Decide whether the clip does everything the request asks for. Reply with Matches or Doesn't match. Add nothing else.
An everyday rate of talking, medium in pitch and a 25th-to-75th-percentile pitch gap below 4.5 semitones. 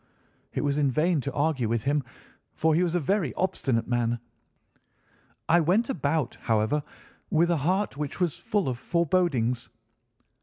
Doesn't match